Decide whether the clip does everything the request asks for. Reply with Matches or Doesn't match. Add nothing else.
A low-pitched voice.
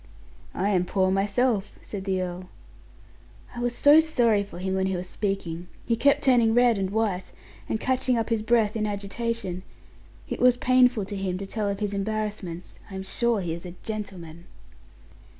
Doesn't match